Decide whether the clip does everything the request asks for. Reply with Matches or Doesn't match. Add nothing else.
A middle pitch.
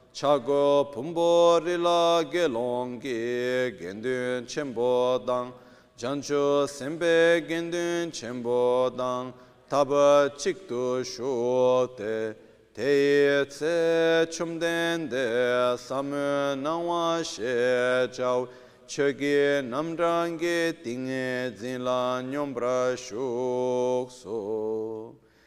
Doesn't match